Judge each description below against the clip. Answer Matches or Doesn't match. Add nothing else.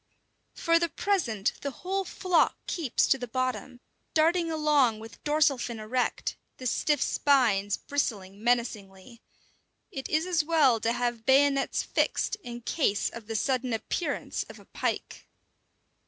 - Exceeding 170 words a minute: Doesn't match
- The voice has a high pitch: Matches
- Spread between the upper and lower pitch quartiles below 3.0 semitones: Doesn't match